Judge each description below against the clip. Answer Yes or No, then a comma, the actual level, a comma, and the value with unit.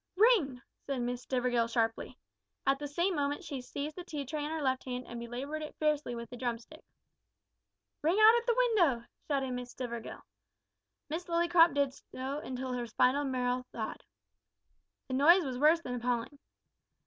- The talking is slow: No, average, 170 wpm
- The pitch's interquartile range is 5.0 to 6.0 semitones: No, average, 4.0 semitones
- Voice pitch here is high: Yes, very high, 275 Hz